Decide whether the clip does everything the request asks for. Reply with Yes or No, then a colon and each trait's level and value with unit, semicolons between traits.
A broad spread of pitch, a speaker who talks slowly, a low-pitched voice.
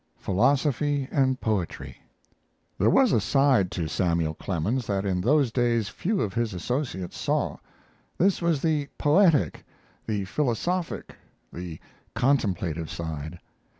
Yes: wide, 7.9 semitones; slow, 120 wpm; low, 115 Hz